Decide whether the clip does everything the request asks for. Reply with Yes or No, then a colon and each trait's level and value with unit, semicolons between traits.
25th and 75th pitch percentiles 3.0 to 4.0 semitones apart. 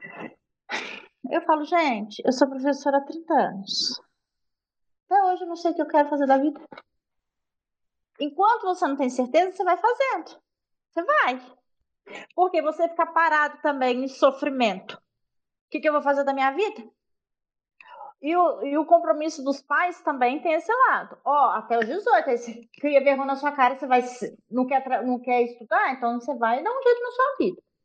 No: average, 4.8 semitones